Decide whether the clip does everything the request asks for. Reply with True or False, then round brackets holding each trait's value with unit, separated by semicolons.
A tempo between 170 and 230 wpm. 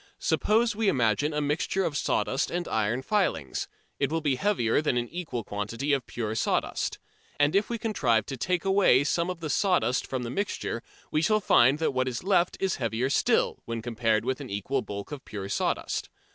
True (200 wpm)